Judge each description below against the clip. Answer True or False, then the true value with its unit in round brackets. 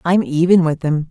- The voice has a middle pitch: True (165 Hz)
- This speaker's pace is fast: True (215 wpm)